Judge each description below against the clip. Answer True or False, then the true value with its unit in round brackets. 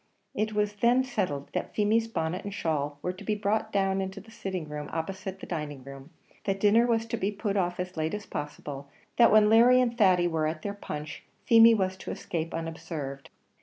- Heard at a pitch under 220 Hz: True (190 Hz)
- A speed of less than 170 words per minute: False (205 wpm)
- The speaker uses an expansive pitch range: False (4.9 semitones)